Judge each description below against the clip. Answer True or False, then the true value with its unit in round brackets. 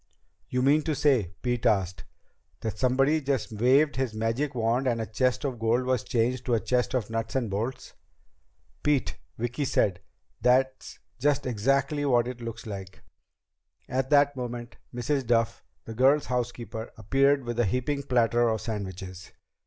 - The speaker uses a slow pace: False (160 wpm)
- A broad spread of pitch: False (2.8 semitones)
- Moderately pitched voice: False (125 Hz)